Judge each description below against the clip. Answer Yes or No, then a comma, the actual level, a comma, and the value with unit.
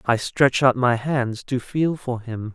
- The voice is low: Yes, low, 125 Hz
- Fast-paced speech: Yes, fast, 215 wpm